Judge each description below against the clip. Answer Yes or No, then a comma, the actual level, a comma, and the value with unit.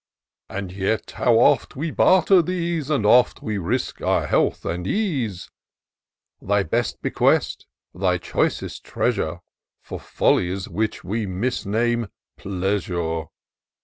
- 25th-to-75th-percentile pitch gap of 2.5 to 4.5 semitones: No, average, 5.2 semitones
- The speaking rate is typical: No, slow, 115 wpm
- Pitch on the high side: No, low, 105 Hz